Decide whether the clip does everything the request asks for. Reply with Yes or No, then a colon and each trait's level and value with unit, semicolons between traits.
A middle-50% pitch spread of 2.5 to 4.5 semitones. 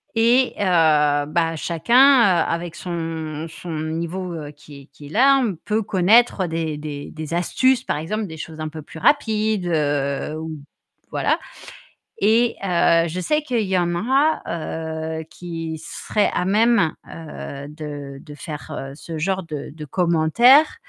No: average, 5.0 semitones